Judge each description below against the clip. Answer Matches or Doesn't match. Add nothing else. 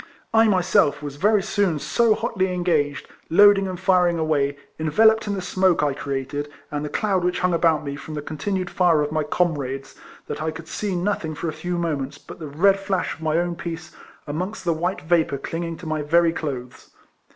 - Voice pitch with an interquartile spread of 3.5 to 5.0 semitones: Matches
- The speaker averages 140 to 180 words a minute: Doesn't match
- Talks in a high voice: Doesn't match